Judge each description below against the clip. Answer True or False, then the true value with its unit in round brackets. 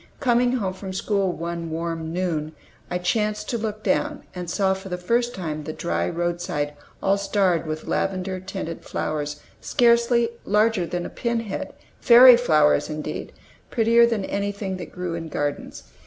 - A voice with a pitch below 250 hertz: True (185 Hz)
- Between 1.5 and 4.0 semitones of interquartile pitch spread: False (4.7 semitones)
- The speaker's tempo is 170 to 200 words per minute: False (160 wpm)